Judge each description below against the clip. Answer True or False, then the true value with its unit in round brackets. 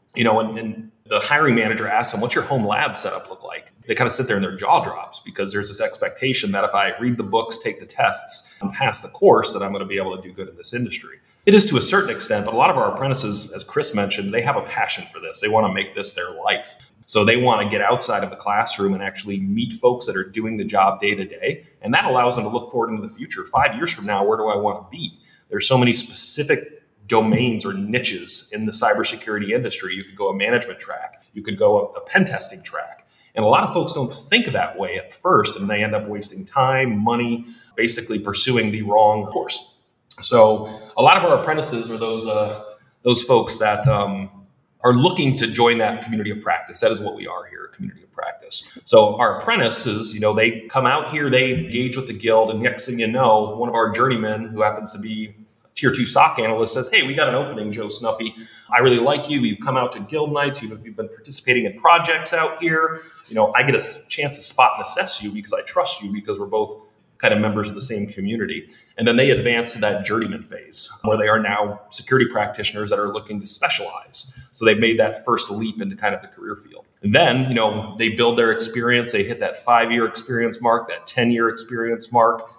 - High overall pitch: False (115 Hz)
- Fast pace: True (240 wpm)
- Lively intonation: False (3.3 semitones)